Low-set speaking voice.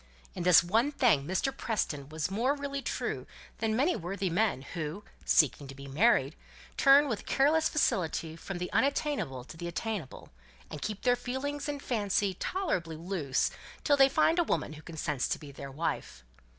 No: high, 195 Hz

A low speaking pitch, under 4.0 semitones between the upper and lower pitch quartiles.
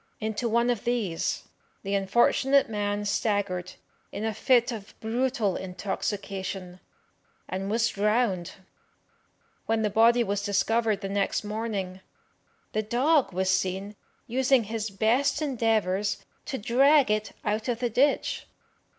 No: high, 215 Hz; average, 3.2 semitones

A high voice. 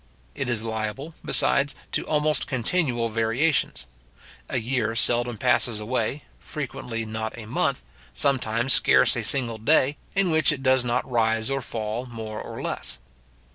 No: low, 120 Hz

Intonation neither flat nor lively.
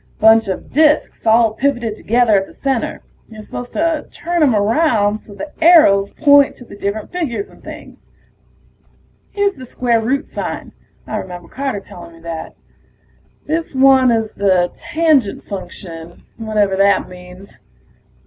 No: wide, 5.8 semitones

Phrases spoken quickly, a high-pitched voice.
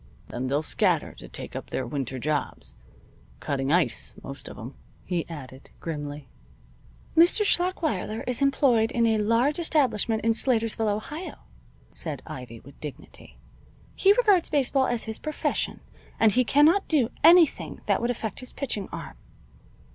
No: average, 145 wpm; high, 225 Hz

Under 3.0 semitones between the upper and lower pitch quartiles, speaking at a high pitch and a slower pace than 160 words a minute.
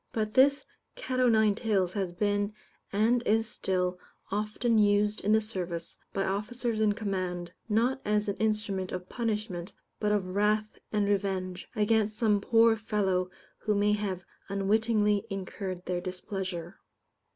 Yes: narrow, 2.4 semitones; high, 210 Hz; average, 145 wpm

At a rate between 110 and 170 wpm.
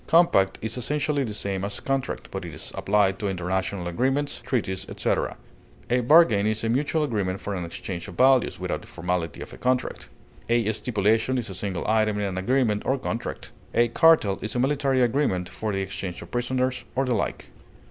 No: average, 190 wpm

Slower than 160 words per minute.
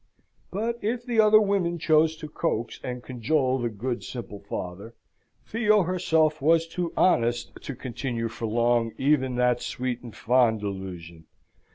Yes: average, 150 wpm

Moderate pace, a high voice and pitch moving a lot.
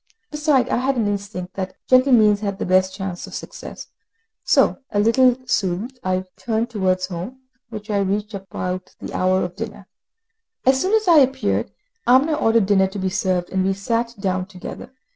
No: average, 180 wpm; high, 205 Hz; average, 4.5 semitones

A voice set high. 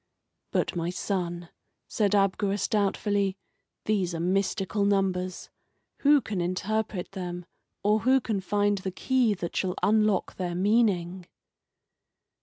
Yes: high, 195 Hz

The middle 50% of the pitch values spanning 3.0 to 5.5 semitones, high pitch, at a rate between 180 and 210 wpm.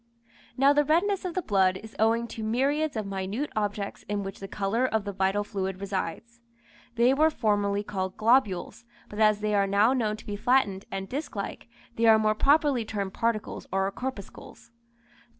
Yes: average, 4.0 semitones; high, 215 Hz; average, 185 wpm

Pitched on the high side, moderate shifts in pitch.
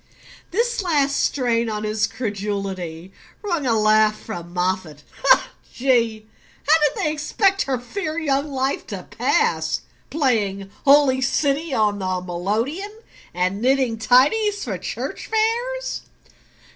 No: very high, 250 Hz; wide, 6.9 semitones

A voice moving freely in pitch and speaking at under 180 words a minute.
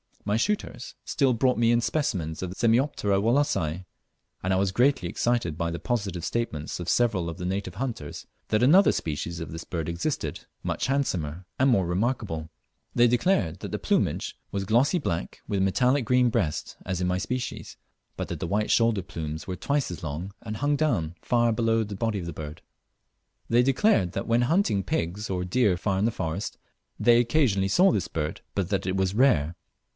No: wide, 5.8 semitones; average, 190 wpm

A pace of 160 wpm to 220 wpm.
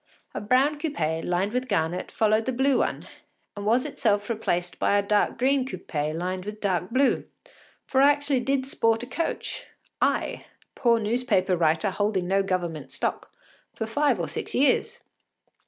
Yes: average, 165 wpm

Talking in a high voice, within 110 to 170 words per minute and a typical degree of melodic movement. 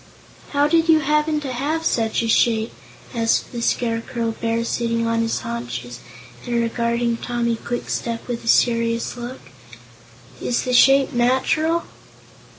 No: high, 235 Hz; average, 140 wpm; narrow, 2.3 semitones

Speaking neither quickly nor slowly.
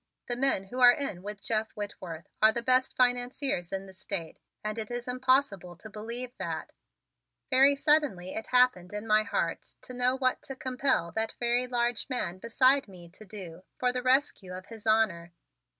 Yes: average, 185 wpm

